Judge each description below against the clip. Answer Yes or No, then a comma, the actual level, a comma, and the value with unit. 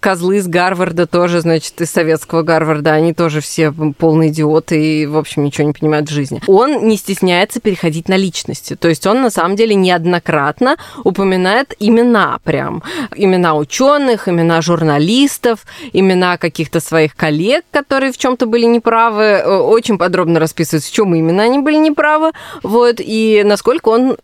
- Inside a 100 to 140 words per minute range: No, fast, 160 wpm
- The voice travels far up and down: Yes, wide, 5.8 semitones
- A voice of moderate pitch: Yes, medium, 180 Hz